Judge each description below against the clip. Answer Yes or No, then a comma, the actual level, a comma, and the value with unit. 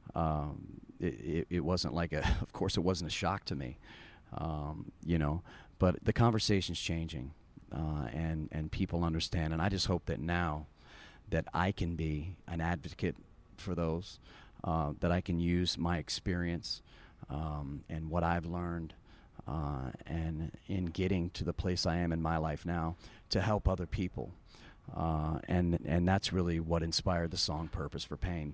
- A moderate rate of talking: Yes, average, 170 wpm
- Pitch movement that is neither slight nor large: No, narrow, 2.2 semitones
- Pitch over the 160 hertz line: No, very low, 85 Hz